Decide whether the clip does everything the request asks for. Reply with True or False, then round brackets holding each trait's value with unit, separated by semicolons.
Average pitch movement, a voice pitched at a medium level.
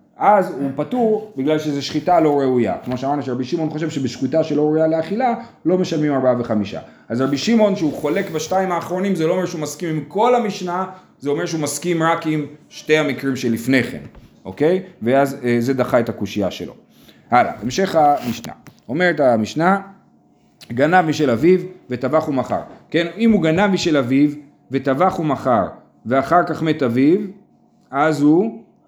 True (5.0 semitones; 155 Hz)